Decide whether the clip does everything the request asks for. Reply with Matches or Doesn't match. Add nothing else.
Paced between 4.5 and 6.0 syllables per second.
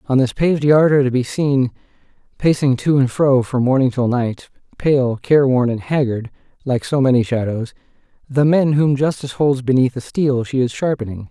Matches